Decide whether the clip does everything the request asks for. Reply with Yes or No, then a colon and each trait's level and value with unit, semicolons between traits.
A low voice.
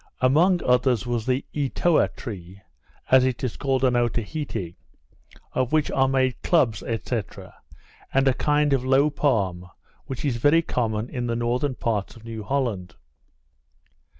Yes: low, 125 Hz